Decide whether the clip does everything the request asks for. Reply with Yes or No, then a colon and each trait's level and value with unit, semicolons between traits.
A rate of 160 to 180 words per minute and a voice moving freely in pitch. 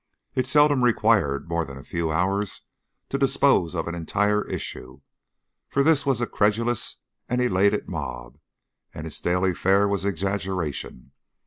No: average, 150 wpm; wide, 6.4 semitones